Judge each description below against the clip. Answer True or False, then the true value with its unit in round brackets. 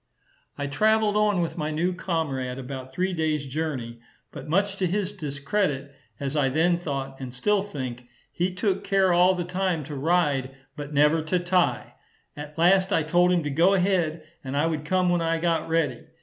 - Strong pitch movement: False (4.4 semitones)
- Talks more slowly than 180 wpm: False (190 wpm)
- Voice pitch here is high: False (165 Hz)